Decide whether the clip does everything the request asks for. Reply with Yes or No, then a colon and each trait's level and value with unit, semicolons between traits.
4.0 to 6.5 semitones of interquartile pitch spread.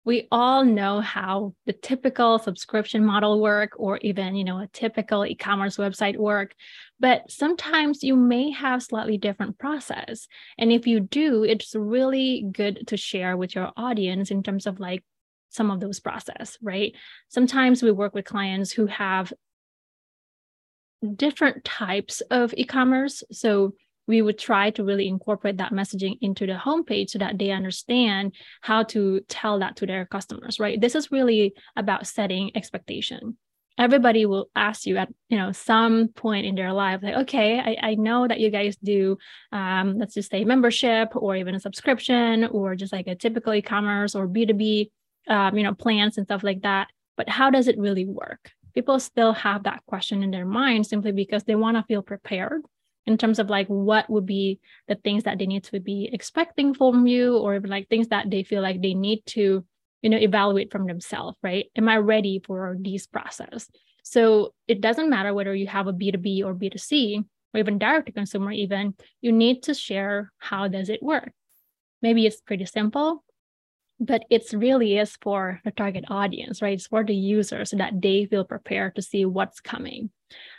No: average, 2.7 semitones